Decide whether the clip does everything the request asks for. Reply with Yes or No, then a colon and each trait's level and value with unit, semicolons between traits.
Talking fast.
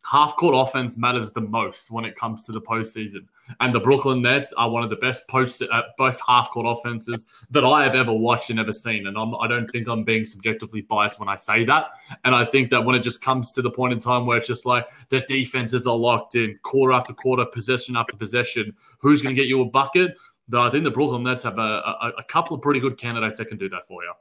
Yes: fast, 255 wpm